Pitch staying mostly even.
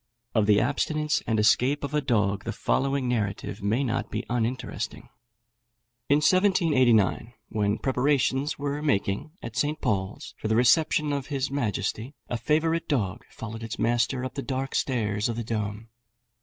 No: average, 4.6 semitones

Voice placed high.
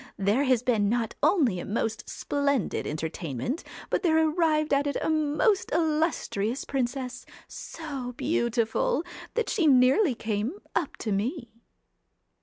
Yes: very high, 260 Hz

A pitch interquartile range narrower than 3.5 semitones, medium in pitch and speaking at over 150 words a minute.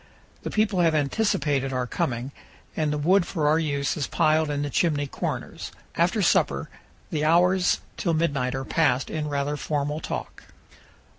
Yes: average, 2.8 semitones; medium, 150 Hz; average, 160 wpm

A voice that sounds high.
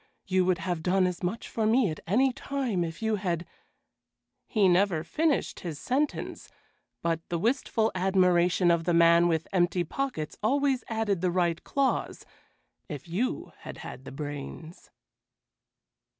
No: medium, 180 Hz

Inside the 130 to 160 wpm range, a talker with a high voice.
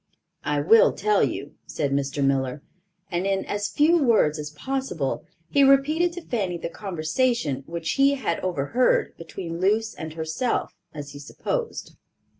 No: average, 150 wpm; medium, 180 Hz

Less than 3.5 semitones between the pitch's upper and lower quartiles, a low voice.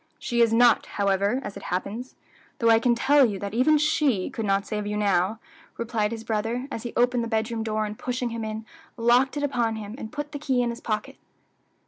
No: average, 2.7 semitones; high, 230 Hz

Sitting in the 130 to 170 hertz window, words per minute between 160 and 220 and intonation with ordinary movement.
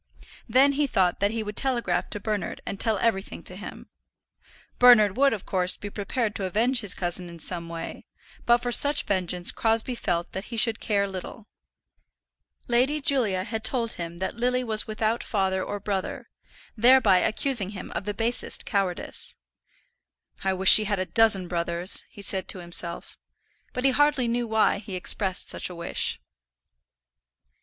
No: high, 210 Hz; average, 170 wpm; average, 4.1 semitones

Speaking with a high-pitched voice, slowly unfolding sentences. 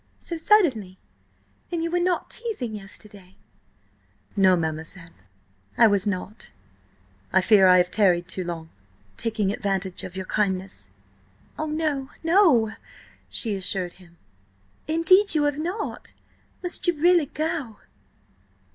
Yes: high, 210 Hz; slow, 120 wpm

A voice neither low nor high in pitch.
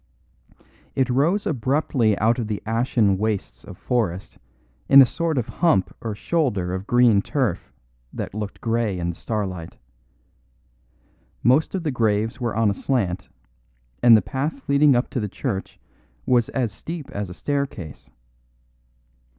No: low, 115 Hz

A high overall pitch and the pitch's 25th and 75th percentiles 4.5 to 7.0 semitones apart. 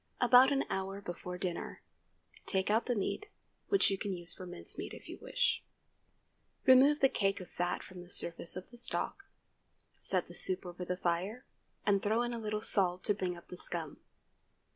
Yes: high, 195 Hz; average, 5.3 semitones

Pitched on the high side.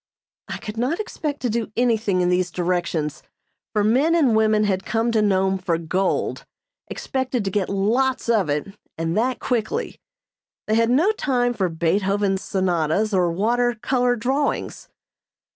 Yes: high, 215 Hz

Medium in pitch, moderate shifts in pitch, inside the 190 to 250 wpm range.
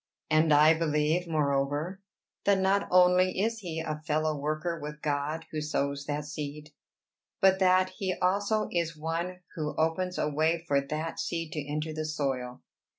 No: medium, 155 Hz; average, 3.2 semitones; average, 160 wpm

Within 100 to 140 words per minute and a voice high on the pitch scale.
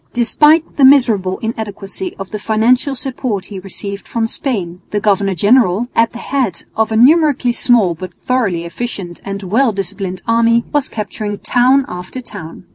No: average, 160 wpm; high, 220 Hz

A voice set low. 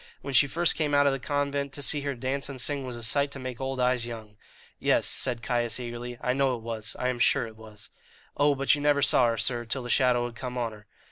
Yes: low, 125 Hz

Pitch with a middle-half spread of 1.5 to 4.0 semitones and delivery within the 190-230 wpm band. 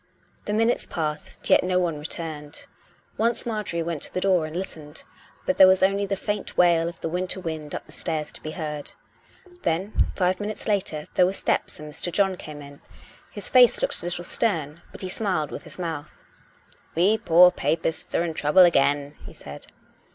Yes: average, 3.6 semitones; average, 195 wpm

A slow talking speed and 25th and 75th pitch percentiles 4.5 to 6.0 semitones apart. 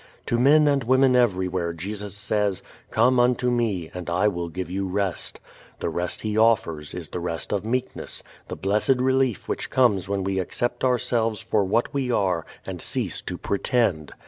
No: average, 175 wpm; average, 4.9 semitones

